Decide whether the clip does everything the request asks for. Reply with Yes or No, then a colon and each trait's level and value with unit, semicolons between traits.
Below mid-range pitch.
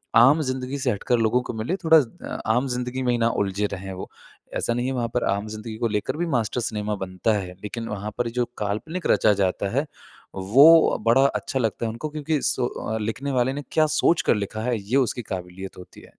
Yes: low, 115 Hz